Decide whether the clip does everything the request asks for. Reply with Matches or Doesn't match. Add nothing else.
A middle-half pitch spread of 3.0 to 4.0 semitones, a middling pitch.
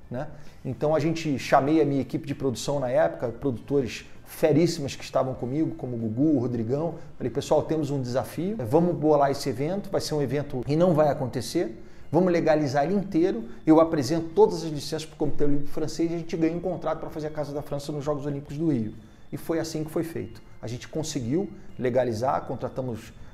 Matches